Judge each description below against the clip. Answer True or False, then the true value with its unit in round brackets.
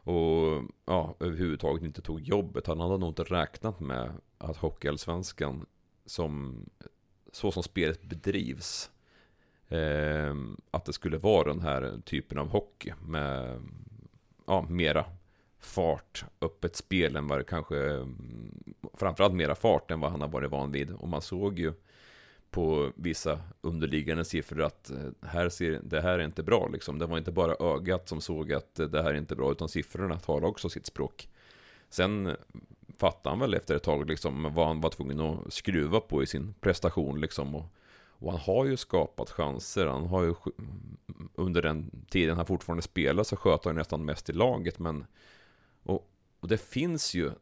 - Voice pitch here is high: False (80 Hz)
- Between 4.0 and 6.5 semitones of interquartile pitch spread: False (3.3 semitones)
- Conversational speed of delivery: True (165 wpm)